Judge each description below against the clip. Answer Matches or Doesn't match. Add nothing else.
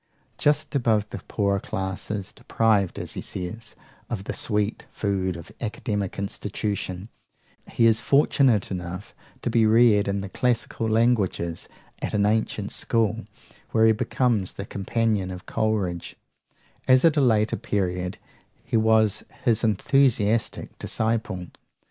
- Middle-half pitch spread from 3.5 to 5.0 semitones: Doesn't match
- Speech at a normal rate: Doesn't match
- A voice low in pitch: Matches